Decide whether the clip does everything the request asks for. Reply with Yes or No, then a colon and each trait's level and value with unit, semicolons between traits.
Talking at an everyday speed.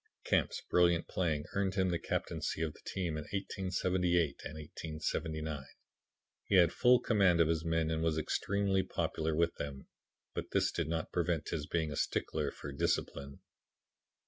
Yes: average, 160 wpm